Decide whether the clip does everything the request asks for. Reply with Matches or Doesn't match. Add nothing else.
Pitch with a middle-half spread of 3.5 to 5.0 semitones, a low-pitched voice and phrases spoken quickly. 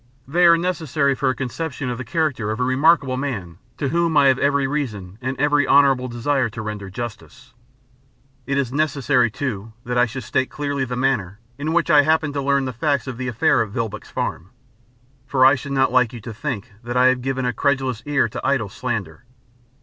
Doesn't match